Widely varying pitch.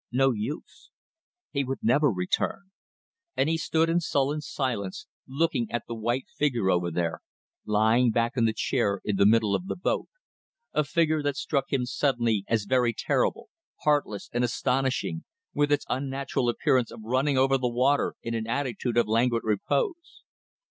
No: average, 3.9 semitones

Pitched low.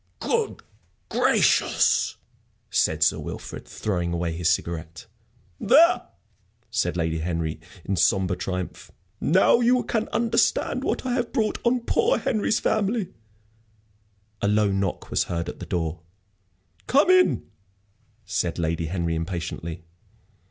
Yes: very low, 95 Hz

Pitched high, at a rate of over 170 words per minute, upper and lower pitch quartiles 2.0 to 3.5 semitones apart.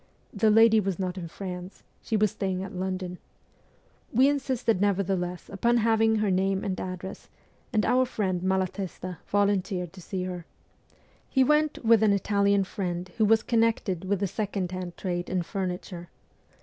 No: high, 195 Hz; average, 160 wpm; average, 2.9 semitones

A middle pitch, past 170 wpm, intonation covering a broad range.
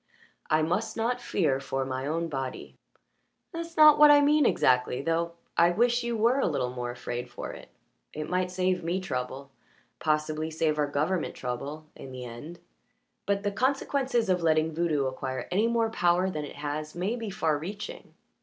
Yes: medium, 165 Hz; average, 180 wpm; wide, 6.5 semitones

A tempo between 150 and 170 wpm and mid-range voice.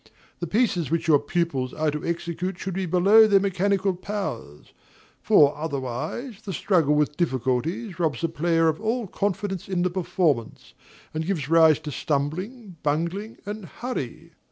Yes: average, 155 wpm; medium, 170 Hz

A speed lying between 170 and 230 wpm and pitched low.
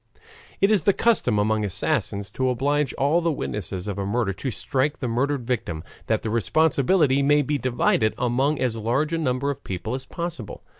Yes: average, 190 wpm; low, 130 Hz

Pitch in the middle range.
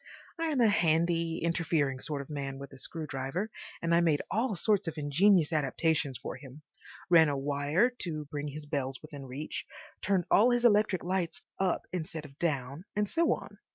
Yes: medium, 160 Hz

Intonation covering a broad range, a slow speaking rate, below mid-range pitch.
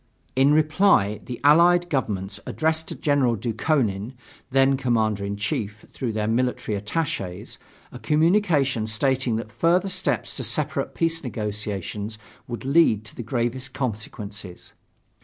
Yes: wide, 5.9 semitones; slow, 130 wpm; low, 120 Hz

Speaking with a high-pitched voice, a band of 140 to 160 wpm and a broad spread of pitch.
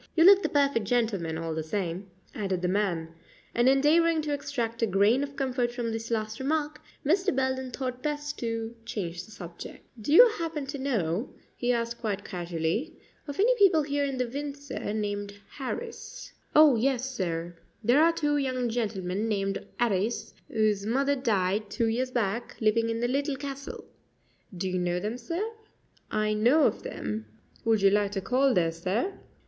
No: high, 235 Hz; average, 175 wpm; wide, 5.7 semitones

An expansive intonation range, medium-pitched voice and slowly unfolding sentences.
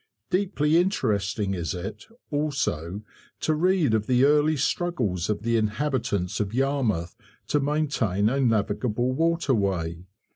No: wide, 6.7 semitones; low, 120 Hz; slow, 120 wpm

